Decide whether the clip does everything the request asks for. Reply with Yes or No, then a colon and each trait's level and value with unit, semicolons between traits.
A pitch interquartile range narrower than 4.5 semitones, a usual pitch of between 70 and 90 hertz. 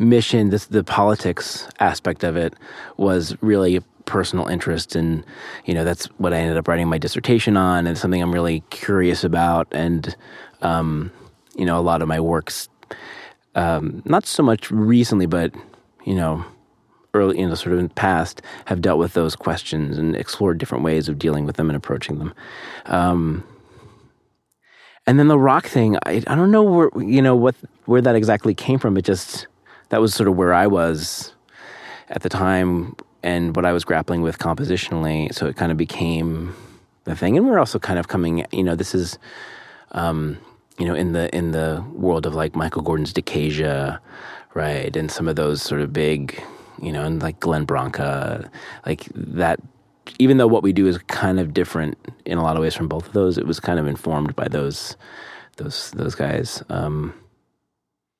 Yes: average, 3.5 semitones; very low, 85 Hz